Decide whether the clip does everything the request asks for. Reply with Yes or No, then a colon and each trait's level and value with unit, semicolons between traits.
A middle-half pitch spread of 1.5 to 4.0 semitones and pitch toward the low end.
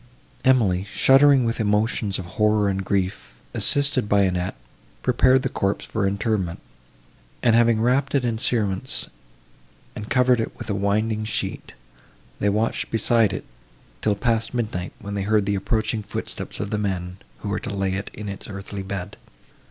Yes: average, 2.9 semitones; low, 105 Hz